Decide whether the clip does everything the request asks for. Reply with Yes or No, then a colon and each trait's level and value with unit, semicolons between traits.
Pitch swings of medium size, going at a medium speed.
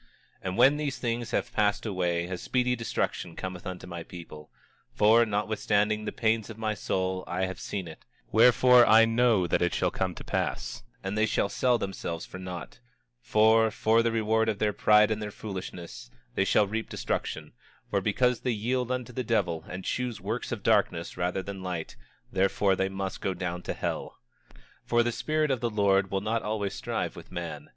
Yes: average, 3.6 semitones; average, 195 wpm